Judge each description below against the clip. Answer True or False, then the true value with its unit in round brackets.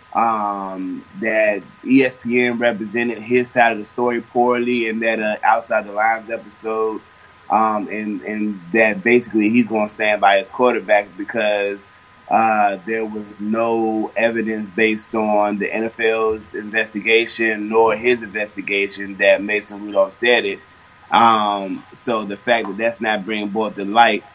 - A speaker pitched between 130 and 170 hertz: False (110 Hz)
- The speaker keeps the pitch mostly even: True (1.8 semitones)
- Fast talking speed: False (145 wpm)